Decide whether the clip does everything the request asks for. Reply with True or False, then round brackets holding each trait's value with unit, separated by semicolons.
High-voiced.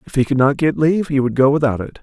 False (140 Hz)